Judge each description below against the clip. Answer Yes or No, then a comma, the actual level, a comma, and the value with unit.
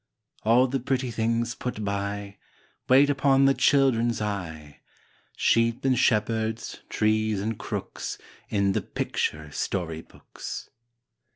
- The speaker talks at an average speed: No, slow, 115 wpm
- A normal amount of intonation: Yes, average, 3.9 semitones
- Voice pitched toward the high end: No, low, 110 Hz